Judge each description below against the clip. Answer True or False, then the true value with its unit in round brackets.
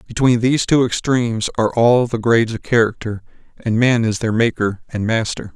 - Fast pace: False (185 wpm)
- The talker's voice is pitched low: True (115 Hz)